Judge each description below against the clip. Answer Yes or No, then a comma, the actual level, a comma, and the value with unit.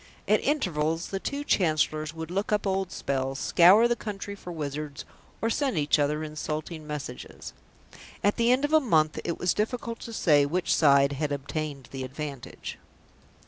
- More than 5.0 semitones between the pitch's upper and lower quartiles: Yes, wide, 5.5 semitones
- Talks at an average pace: Yes, average, 170 wpm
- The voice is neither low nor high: Yes, medium, 160 Hz